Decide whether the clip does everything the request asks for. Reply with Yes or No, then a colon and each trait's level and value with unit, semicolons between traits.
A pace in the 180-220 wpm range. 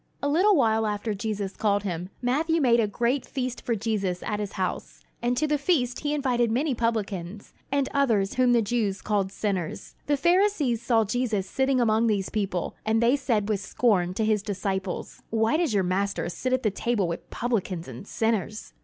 Yes: average, 190 wpm